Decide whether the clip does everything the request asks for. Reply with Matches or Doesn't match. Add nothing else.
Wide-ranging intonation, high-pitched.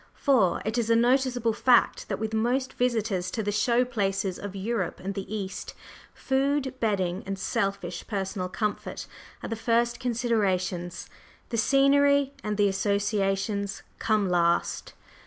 Doesn't match